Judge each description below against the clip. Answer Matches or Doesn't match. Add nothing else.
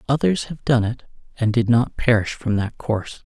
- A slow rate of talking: Doesn't match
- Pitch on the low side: Matches